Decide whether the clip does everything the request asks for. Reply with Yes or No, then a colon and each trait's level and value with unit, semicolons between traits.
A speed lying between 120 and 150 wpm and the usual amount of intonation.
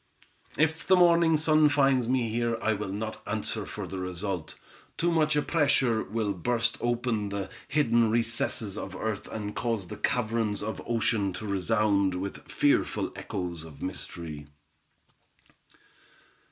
Yes: average, 140 wpm; average, 3.9 semitones